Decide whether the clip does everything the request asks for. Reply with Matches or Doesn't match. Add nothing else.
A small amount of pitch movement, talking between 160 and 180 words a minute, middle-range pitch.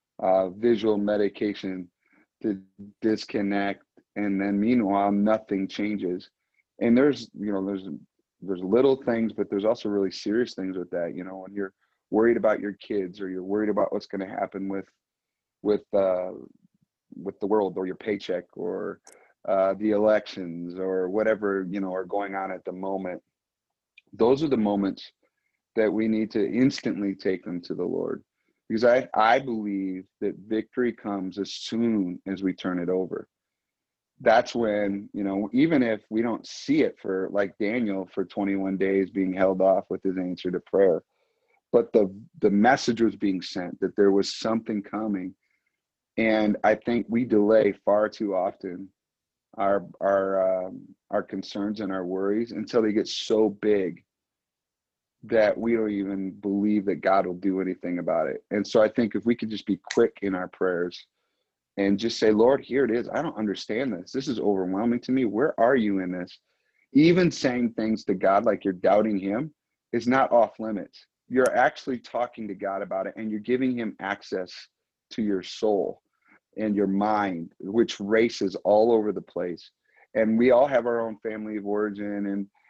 Doesn't match